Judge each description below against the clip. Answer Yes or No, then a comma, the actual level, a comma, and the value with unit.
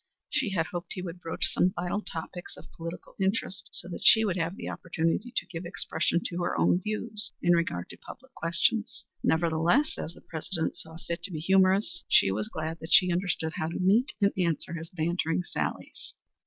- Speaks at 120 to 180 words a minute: No, average, 195 wpm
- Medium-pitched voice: Yes, medium, 175 Hz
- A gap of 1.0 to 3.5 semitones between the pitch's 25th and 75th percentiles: Yes, average, 2.8 semitones